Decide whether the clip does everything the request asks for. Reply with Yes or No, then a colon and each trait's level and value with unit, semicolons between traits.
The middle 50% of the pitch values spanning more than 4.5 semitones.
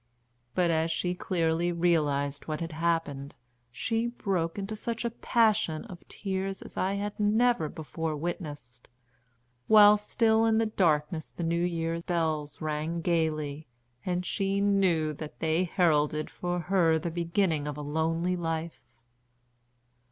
No: average, 3.6 semitones